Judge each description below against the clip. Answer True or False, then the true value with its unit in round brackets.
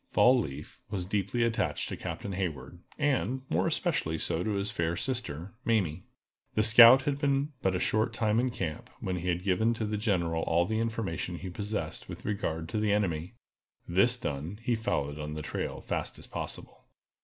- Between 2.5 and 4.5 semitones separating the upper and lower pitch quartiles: False (5.3 semitones)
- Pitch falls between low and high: False (100 Hz)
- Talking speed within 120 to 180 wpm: False (190 wpm)